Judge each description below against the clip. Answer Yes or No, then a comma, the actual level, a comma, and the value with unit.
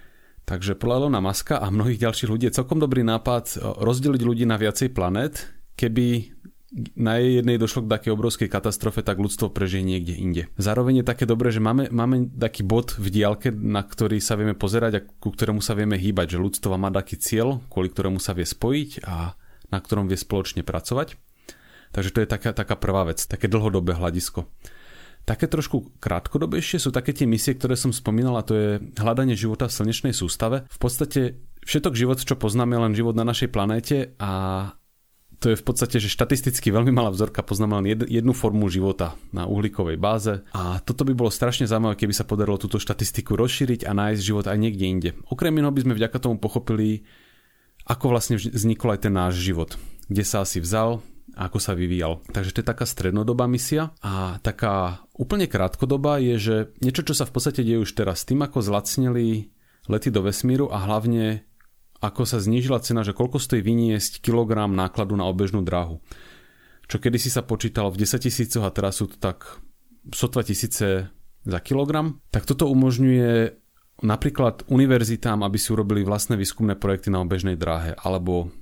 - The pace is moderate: No, fast, 180 wpm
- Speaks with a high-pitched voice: No, low, 110 Hz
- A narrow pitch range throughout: No, average, 3.6 semitones